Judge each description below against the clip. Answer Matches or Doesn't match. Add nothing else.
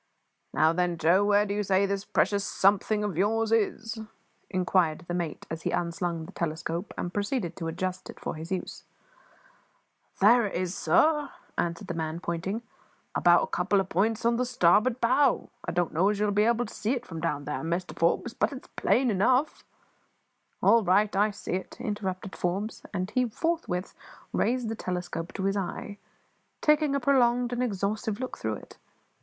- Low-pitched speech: Doesn't match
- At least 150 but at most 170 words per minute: Doesn't match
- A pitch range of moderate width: Matches